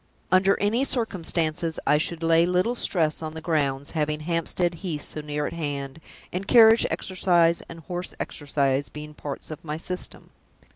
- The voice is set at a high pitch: No, medium, 165 Hz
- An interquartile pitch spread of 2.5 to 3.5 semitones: Yes, average, 3.1 semitones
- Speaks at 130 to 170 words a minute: Yes, average, 160 wpm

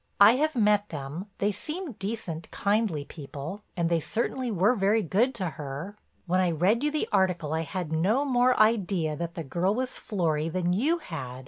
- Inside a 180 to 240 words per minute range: Yes, average, 190 wpm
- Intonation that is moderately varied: No, wide, 5.7 semitones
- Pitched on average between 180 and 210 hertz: Yes, high, 190 Hz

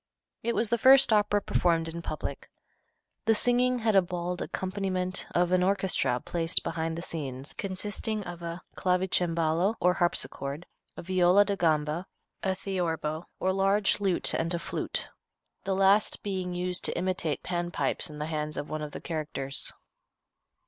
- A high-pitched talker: No, medium, 180 Hz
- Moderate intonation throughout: Yes, average, 3.0 semitones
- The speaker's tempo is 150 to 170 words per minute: Yes, average, 160 wpm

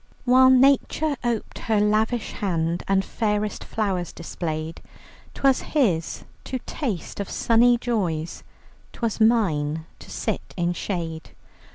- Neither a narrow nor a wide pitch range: No, wide, 6.0 semitones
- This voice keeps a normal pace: No, slow, 115 wpm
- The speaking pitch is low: No, high, 210 Hz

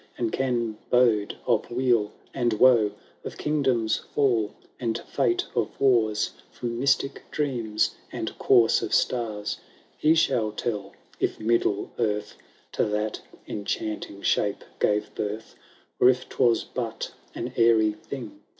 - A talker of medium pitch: No, low, 115 Hz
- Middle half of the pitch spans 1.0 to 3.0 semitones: Yes, average, 2.7 semitones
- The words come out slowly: Yes, slow, 130 wpm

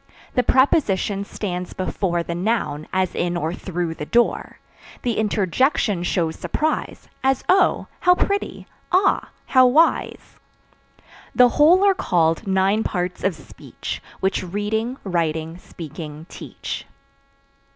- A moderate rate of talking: No, slow, 120 wpm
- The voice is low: No, high, 195 Hz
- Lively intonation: Yes, wide, 6.3 semitones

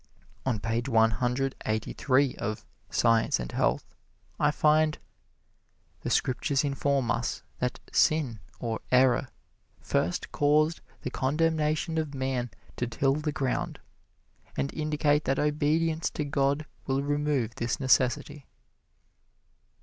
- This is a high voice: No, low, 135 Hz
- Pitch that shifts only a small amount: No, average, 3.4 semitones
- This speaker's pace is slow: Yes, slow, 120 wpm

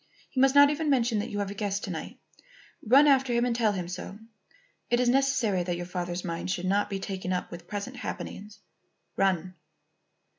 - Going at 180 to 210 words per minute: Yes, average, 200 wpm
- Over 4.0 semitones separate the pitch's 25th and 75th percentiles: Yes, average, 5.2 semitones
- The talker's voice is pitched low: No, high, 205 Hz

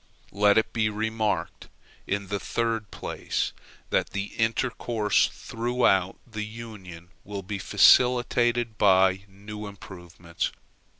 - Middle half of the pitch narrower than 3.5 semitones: Yes, narrow, 2.6 semitones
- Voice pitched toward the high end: No, low, 105 Hz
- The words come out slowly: Yes, slow, 110 wpm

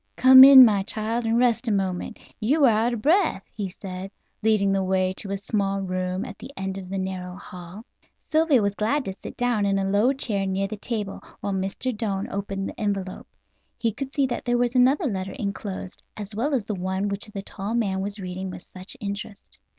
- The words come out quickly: Yes, fast, 215 wpm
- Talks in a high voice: Yes, high, 200 Hz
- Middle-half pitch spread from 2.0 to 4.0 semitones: Yes, average, 3.6 semitones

